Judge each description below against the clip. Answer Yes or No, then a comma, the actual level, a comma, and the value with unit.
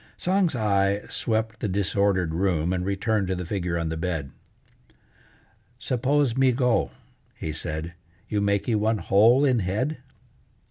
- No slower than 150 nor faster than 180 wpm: No, average, 140 wpm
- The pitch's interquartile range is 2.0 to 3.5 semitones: No, average, 4.5 semitones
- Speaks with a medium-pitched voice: No, low, 100 Hz